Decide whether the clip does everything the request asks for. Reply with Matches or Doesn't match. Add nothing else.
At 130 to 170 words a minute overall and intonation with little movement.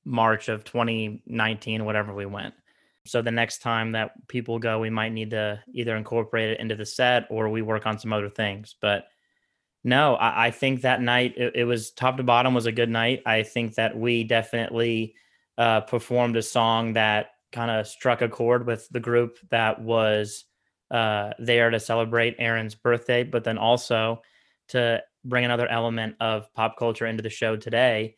Doesn't match